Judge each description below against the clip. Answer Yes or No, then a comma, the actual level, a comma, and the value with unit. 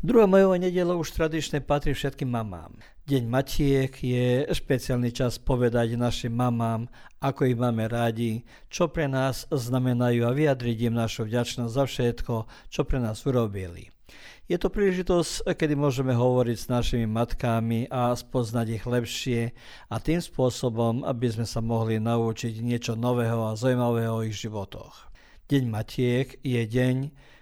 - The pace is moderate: Yes, average, 145 wpm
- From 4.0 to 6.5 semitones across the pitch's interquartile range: No, average, 2.8 semitones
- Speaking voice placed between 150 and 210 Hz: No, low, 125 Hz